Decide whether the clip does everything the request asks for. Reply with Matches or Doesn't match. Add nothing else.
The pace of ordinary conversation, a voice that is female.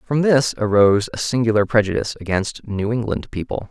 Doesn't match